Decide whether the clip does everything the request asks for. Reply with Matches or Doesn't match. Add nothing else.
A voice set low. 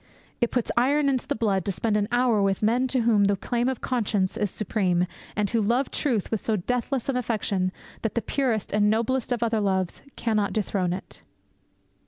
Doesn't match